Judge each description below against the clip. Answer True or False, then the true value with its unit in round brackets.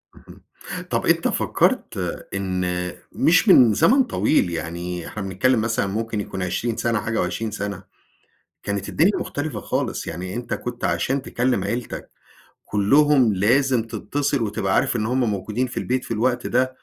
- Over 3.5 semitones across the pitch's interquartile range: True (4.5 semitones)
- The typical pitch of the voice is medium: False (110 Hz)